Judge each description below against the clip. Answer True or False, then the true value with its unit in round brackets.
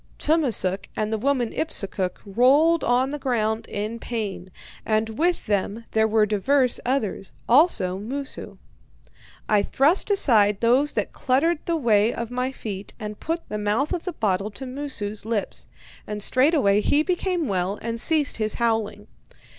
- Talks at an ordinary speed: True (155 wpm)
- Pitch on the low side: False (230 Hz)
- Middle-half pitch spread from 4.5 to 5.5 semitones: True (5.2 semitones)